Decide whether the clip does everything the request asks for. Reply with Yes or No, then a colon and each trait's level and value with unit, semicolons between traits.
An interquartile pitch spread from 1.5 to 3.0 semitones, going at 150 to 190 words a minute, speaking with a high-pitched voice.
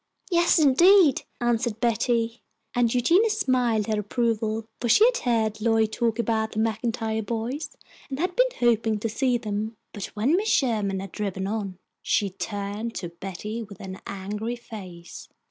Yes: average, 2.7 semitones; average, 160 wpm; high, 225 Hz